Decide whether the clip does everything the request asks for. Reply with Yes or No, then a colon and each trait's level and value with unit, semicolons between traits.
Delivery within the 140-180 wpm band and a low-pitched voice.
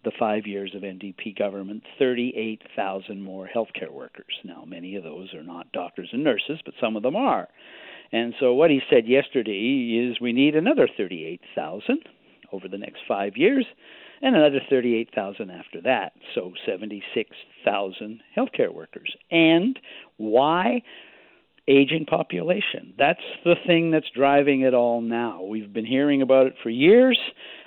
Yes: average, 145 wpm; low, 130 Hz